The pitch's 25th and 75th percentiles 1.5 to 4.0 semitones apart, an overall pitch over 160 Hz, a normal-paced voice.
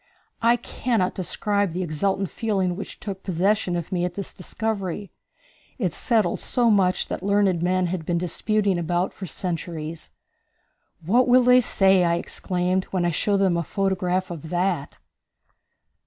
Yes: narrow, 2.6 semitones; medium, 185 Hz; average, 155 wpm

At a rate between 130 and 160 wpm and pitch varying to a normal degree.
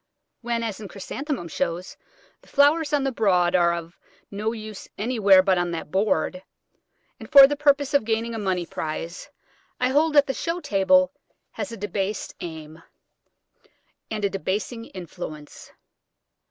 No: average, 155 wpm; wide, 7.0 semitones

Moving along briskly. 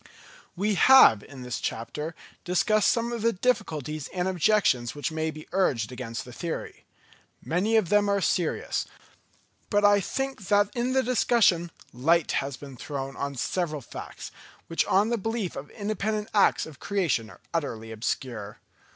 No: average, 160 wpm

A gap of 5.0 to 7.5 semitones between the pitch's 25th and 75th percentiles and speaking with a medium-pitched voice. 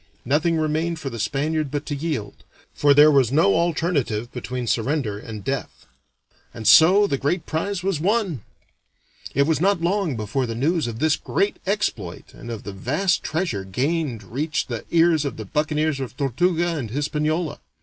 Yes: average, 5.3 semitones; medium, 150 Hz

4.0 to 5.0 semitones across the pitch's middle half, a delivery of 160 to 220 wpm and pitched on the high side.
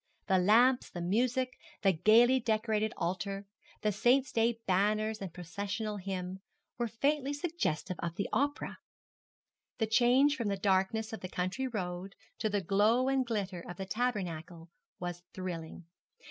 No: average, 4.6 semitones; average, 145 wpm; high, 210 Hz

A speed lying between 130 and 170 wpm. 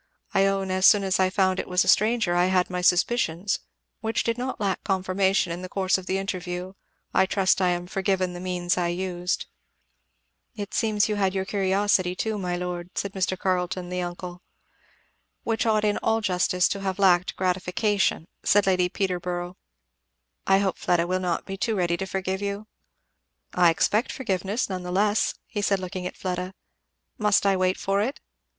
No: average, 180 wpm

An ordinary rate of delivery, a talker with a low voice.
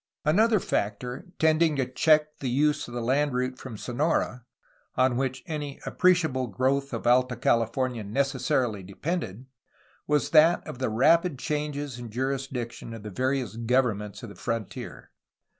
Yes: average, 150 wpm; low, 130 Hz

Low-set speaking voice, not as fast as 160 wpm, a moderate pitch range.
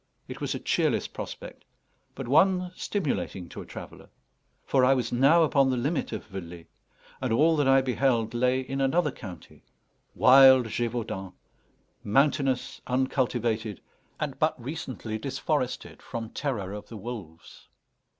Yes: low, 130 Hz; average, 140 wpm; average, 3.5 semitones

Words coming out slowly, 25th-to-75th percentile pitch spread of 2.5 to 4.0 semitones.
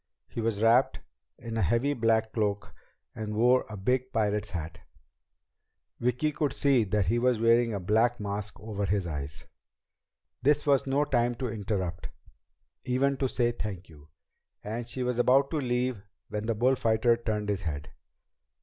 No: average, 160 wpm; average, 3.3 semitones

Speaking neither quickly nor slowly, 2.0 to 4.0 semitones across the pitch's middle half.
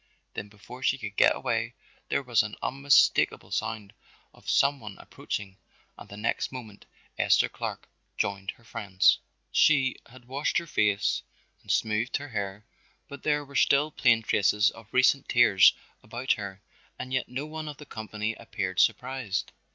No: average, 160 wpm; average, 4.5 semitones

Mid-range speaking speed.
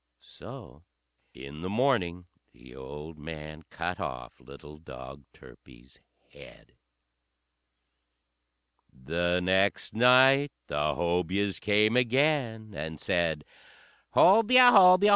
No: slow, 95 wpm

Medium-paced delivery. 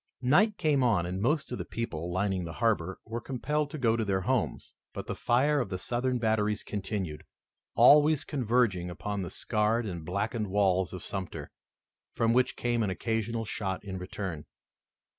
Yes: average, 175 wpm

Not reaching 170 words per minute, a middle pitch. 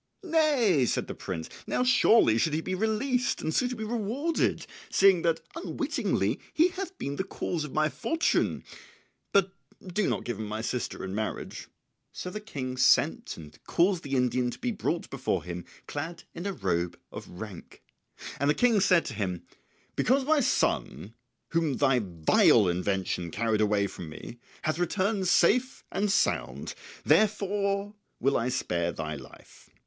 Yes: average, 160 wpm; medium, 160 Hz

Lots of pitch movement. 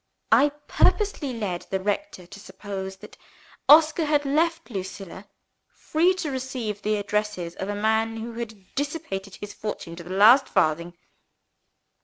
Yes: wide, 6.5 semitones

